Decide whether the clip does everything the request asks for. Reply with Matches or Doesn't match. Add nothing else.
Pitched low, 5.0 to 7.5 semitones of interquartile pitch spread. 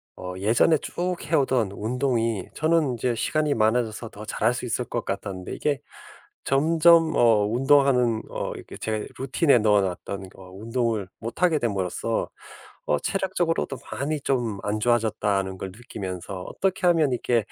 Matches